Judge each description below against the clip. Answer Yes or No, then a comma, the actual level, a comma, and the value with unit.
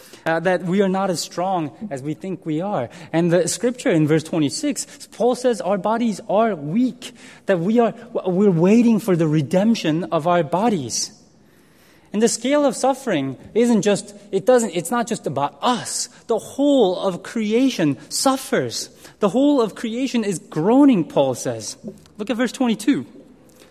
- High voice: Yes, high, 200 Hz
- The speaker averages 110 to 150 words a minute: No, average, 165 wpm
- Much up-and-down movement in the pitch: Yes, wide, 6.0 semitones